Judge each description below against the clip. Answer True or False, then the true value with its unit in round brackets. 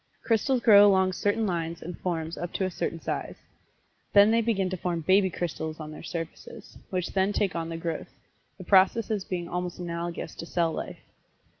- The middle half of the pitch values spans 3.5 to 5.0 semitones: False (3.1 semitones)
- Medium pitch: True (180 Hz)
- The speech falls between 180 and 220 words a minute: True (185 wpm)